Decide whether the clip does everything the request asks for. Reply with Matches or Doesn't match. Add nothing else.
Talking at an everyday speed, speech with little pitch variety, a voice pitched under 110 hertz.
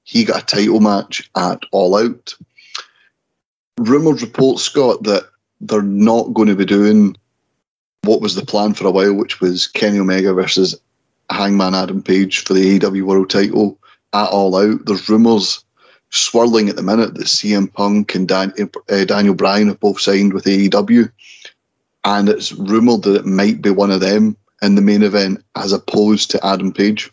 Matches